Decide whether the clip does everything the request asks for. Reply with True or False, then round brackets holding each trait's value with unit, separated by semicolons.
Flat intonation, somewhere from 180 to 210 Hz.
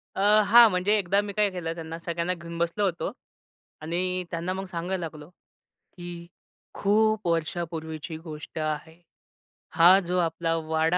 False (2.2 semitones; 170 Hz)